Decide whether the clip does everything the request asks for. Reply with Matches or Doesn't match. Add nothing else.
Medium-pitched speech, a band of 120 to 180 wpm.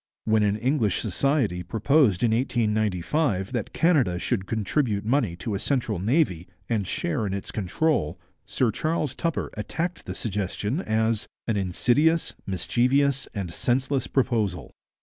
Doesn't match